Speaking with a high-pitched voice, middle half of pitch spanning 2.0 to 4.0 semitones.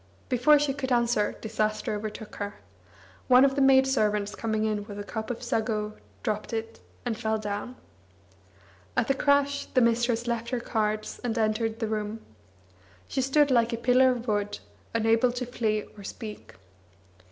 Yes: high, 225 Hz; average, 2.7 semitones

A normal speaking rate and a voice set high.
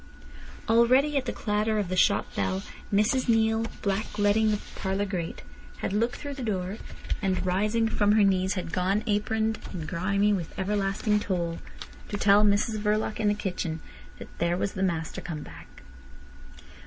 Yes: average, 165 wpm; high, 205 Hz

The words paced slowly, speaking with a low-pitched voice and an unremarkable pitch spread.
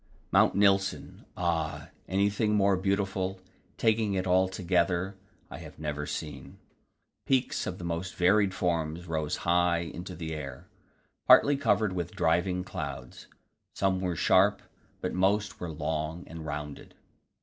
Yes: slow, 130 wpm; very low, 90 Hz; average, 3.1 semitones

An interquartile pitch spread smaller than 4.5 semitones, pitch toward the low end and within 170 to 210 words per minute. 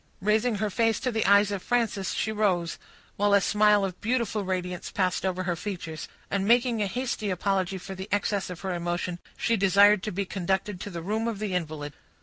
No: narrow, 2.6 semitones; high, 200 Hz; fast, 205 wpm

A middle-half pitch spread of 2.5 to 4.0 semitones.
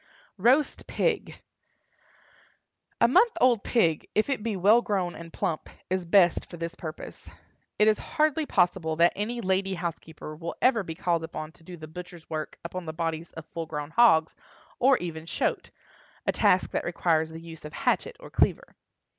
No: average, 4.6 semitones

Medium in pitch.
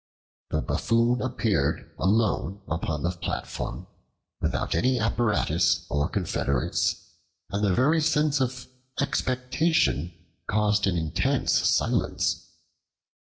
No: low, 110 Hz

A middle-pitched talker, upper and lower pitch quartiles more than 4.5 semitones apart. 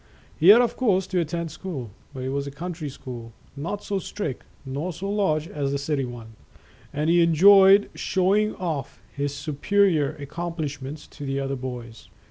Yes: medium, 155 Hz; average, 5.1 semitones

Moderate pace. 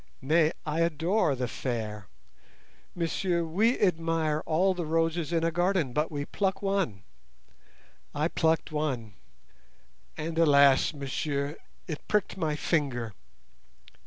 No: slow, 120 wpm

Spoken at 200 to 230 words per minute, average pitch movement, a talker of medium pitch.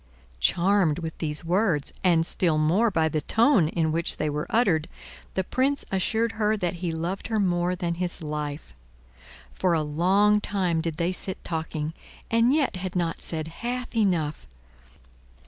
No: average, 165 wpm; average, 4.3 semitones; medium, 175 Hz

